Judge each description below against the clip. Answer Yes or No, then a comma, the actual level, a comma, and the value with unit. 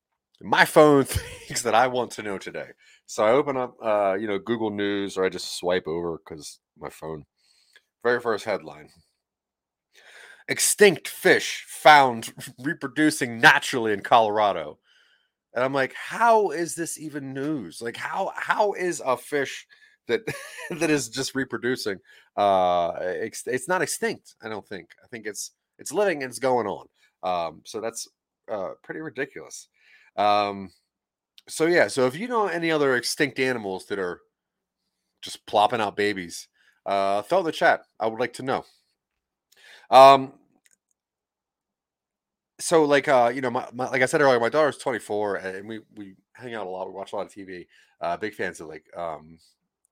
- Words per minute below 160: No, average, 165 wpm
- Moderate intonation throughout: No, wide, 7.1 semitones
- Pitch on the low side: Yes, low, 130 Hz